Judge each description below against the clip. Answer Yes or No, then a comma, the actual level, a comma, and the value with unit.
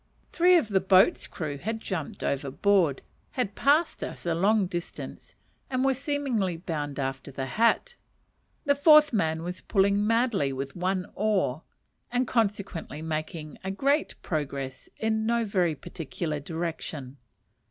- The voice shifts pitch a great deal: Yes, wide, 6.7 semitones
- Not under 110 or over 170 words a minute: Yes, slow, 135 wpm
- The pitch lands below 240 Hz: Yes, high, 190 Hz